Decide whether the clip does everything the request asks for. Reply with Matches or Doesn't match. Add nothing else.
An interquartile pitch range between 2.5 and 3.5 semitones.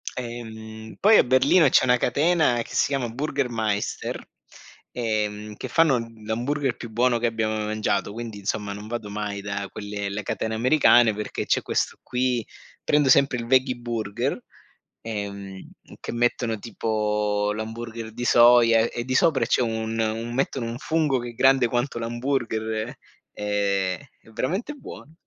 Matches